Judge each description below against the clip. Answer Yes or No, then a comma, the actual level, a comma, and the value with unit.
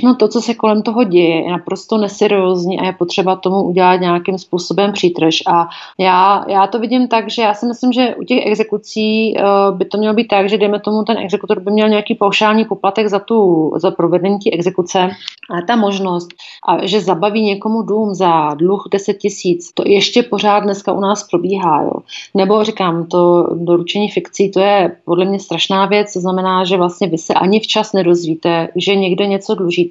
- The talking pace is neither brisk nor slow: No, fast, 195 wpm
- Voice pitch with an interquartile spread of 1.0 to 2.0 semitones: No, narrow, 2.6 semitones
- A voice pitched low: No, high, 195 Hz